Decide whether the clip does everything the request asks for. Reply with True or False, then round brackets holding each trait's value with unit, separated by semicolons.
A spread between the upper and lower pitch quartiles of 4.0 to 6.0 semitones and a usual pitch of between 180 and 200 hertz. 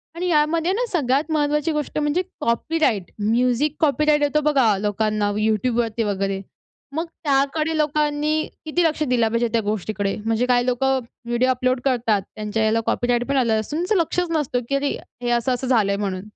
False (5.2 semitones; 255 Hz)